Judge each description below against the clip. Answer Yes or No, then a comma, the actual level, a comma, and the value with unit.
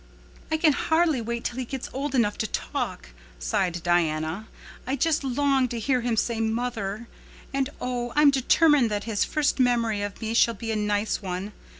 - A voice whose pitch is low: No, high, 235 Hz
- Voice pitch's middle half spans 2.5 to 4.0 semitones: No, average, 4.4 semitones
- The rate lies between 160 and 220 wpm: Yes, average, 185 wpm